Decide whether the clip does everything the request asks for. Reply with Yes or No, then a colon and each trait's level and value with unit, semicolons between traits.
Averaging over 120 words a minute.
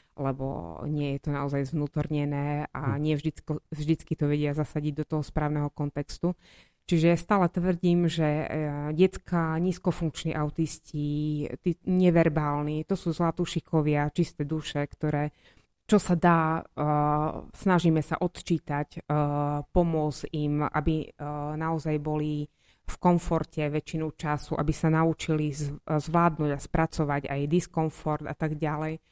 No: average, 115 wpm